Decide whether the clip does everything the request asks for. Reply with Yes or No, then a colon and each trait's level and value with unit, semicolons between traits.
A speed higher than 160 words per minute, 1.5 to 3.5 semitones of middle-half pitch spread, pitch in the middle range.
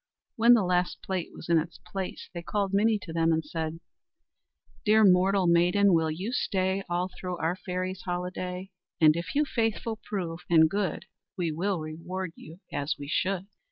Yes: average, 175 wpm; average, 2.9 semitones; medium, 180 Hz